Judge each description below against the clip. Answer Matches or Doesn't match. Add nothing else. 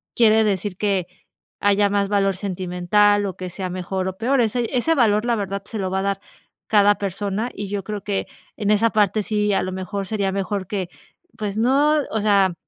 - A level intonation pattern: Matches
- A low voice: Doesn't match